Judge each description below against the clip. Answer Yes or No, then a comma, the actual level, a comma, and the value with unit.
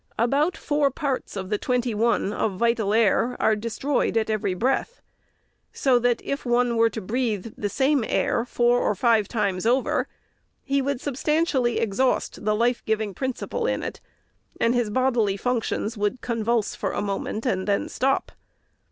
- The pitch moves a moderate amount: Yes, average, 3.4 semitones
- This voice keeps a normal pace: Yes, average, 170 wpm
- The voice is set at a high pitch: Yes, high, 235 Hz